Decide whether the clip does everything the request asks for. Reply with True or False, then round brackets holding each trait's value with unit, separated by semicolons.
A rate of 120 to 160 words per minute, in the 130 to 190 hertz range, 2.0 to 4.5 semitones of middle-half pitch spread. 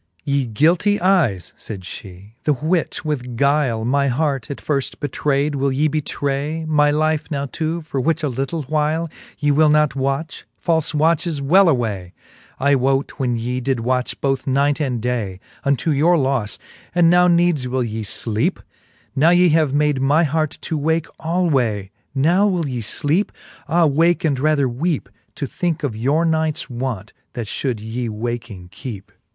False (170 wpm; 140 Hz; 4.1 semitones)